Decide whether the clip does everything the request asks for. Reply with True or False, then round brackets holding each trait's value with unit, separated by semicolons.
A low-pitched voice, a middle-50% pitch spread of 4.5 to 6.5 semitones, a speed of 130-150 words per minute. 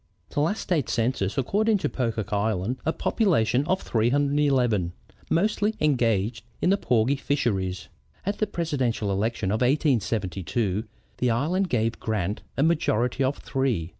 True (125 Hz; 5.5 semitones; 135 wpm)